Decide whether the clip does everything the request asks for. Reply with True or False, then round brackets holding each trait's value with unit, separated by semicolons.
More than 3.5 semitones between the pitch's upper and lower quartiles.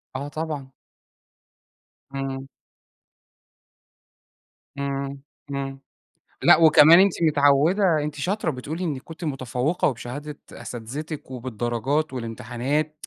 False (2.8 semitones)